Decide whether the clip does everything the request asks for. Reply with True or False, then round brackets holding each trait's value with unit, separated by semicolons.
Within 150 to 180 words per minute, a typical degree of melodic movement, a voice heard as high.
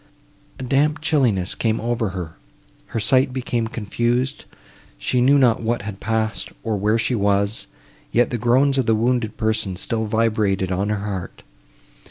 False (160 wpm; 3.1 semitones; 115 Hz)